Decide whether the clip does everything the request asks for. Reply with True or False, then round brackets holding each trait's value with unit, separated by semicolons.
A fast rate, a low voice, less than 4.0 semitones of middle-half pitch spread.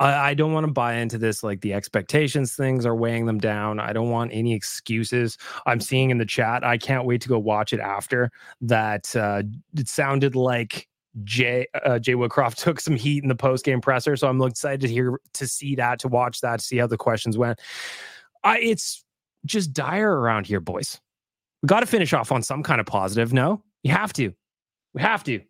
True (215 wpm; 125 Hz; 3.4 semitones)